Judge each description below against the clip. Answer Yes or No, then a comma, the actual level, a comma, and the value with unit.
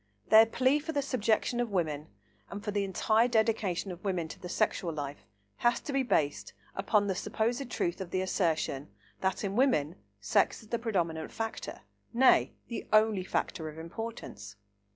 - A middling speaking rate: Yes, average, 170 wpm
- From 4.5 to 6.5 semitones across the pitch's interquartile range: Yes, average, 5.1 semitones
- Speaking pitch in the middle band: No, high, 205 Hz